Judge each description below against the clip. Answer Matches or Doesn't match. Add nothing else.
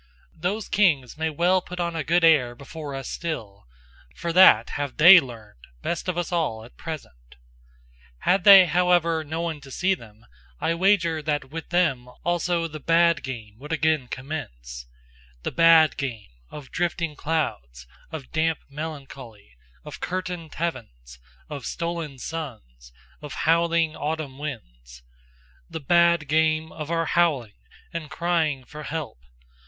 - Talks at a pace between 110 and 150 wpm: Matches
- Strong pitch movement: Doesn't match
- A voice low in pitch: Doesn't match